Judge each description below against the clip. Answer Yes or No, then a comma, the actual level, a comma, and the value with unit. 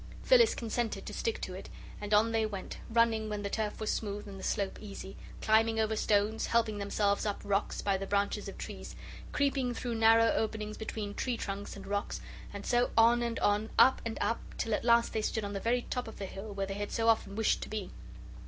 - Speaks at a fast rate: Yes, fast, 225 wpm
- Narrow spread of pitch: Yes, narrow, 2.0 semitones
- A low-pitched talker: No, high, 215 Hz